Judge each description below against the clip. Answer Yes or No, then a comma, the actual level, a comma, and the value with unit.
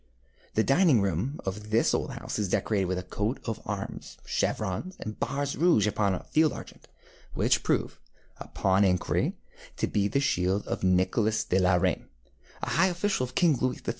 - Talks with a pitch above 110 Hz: No, low, 105 Hz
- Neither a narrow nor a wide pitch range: No, wide, 6.3 semitones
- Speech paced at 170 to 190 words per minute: Yes, average, 180 wpm